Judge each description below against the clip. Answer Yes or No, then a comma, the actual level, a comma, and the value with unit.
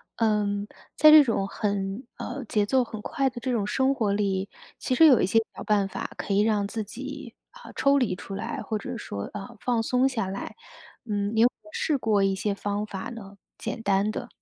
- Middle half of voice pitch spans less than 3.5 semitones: No, average, 3.8 semitones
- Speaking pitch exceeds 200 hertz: Yes, high, 215 Hz